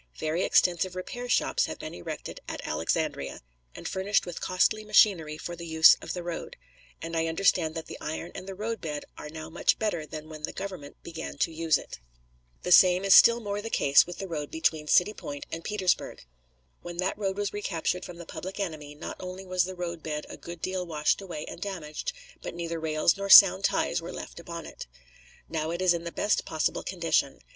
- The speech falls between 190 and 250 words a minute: Yes, fast, 205 wpm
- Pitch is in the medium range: Yes, medium, 170 Hz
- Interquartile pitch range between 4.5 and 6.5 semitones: No, average, 3.0 semitones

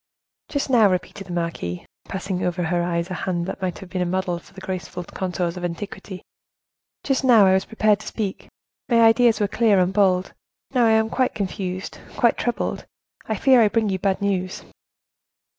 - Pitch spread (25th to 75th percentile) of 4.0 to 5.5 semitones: No, average, 3.4 semitones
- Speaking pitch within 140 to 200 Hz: Yes, high, 190 Hz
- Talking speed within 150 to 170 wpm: No, average, 195 wpm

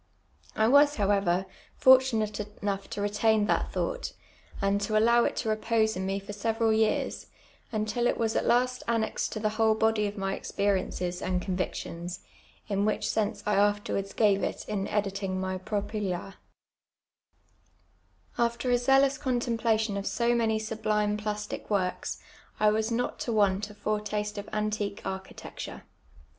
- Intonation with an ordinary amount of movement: No, narrow, 2.0 semitones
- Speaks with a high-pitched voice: Yes, high, 210 Hz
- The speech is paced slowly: No, average, 160 wpm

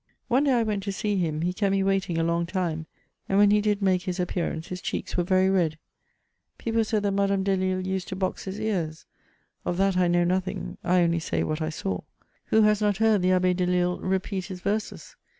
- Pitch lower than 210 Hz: Yes, medium, 185 Hz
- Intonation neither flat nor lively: No, narrow, 2.2 semitones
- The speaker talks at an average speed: No, fast, 220 wpm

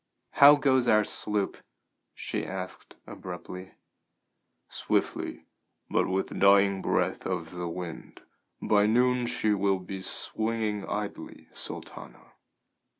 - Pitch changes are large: No, average, 2.8 semitones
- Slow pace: Yes, slow, 110 wpm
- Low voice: Yes, low, 100 Hz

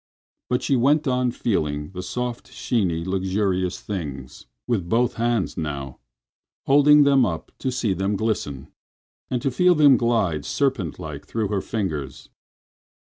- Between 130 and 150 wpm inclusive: Yes, slow, 135 wpm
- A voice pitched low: Yes, low, 105 Hz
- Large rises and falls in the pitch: Yes, wide, 6.4 semitones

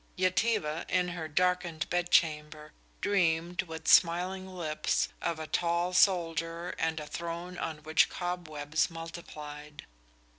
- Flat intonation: Yes, narrow, 2.3 semitones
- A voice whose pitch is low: No, medium, 170 Hz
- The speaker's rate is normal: No, slow, 120 wpm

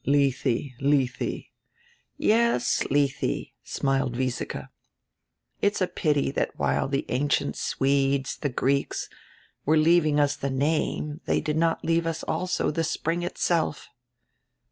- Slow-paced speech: Yes, slow, 120 wpm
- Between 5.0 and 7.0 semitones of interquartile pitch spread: No, average, 3.1 semitones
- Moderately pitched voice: Yes, medium, 145 Hz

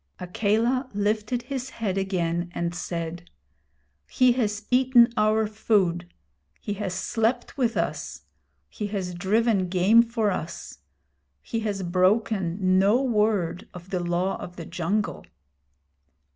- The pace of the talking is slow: Yes, slow, 125 wpm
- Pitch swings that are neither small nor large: Yes, average, 4.0 semitones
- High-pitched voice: Yes, high, 205 Hz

